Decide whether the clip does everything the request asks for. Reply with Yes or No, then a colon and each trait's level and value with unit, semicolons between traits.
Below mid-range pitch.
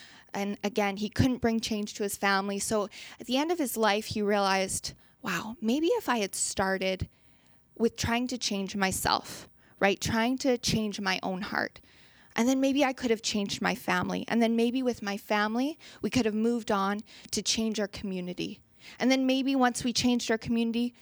No: high, 220 Hz